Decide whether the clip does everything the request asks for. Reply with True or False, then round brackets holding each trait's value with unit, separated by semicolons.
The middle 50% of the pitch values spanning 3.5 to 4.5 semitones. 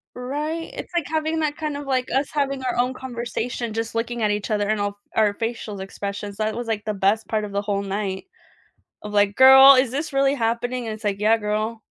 True (4.2 semitones)